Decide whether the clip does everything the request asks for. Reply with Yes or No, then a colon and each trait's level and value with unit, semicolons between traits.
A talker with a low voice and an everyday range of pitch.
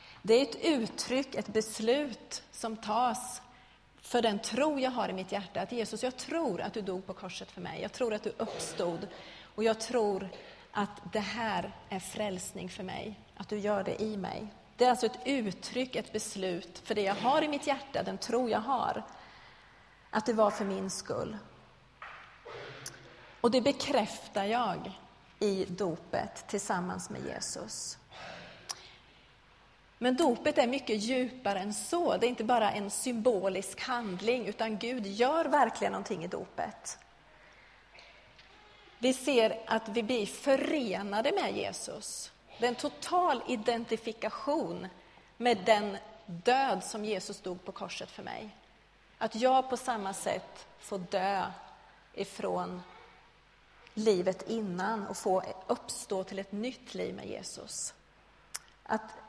No: high, 220 Hz; average, 3.8 semitones